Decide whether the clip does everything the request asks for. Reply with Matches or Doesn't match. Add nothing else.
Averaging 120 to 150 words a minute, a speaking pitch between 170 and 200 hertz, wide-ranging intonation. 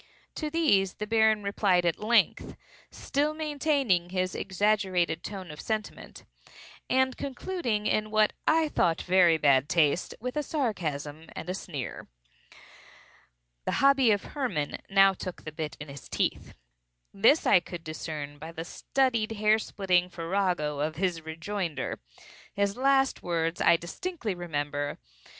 Matches